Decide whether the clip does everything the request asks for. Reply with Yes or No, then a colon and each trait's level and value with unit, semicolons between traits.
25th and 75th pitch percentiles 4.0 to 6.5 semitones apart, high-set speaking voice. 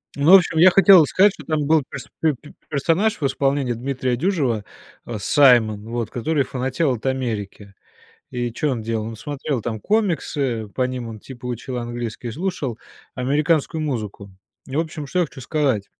No: average, 4.6 semitones; low, 130 Hz